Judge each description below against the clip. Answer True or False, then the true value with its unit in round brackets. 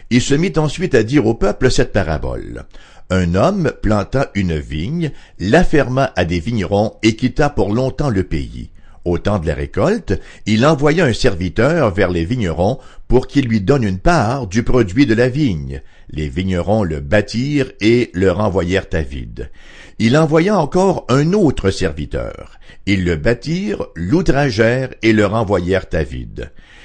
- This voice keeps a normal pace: True (165 wpm)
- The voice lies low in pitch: True (110 Hz)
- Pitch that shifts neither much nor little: False (6.9 semitones)